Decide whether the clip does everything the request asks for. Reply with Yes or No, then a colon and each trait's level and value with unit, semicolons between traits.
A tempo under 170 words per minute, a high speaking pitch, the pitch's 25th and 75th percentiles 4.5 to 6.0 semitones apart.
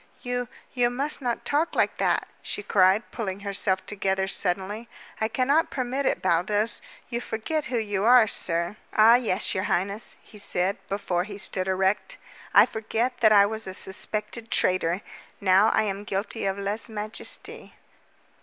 No: average, 160 wpm; high, 210 Hz; average, 3.6 semitones